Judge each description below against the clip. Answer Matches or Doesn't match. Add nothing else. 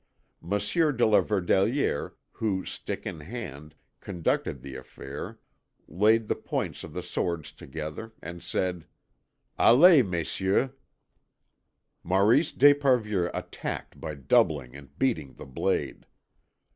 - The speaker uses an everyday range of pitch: Doesn't match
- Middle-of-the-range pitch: Doesn't match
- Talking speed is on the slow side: Matches